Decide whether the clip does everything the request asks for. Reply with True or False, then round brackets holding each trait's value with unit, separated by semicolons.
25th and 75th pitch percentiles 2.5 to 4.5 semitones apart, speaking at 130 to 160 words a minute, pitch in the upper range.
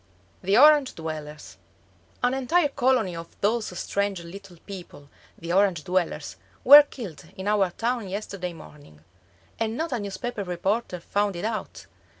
False (5.4 semitones; 150 wpm; 200 Hz)